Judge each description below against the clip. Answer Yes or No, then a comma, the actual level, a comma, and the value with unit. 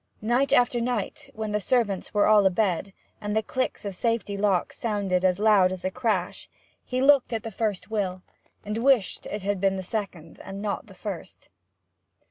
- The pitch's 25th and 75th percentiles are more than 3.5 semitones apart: No, average, 3.1 semitones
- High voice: Yes, high, 210 Hz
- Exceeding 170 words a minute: Yes, average, 185 wpm